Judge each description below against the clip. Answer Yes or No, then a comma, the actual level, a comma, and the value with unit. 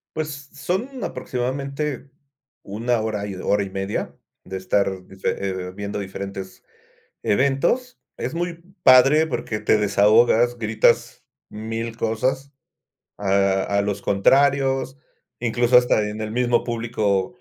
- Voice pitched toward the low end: Yes, low, 115 Hz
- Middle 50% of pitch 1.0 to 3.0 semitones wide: No, average, 4.8 semitones